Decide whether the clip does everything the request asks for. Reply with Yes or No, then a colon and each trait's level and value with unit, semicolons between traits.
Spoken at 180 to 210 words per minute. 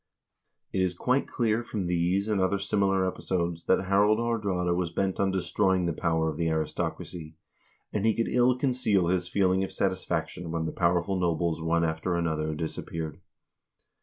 No: average, 165 wpm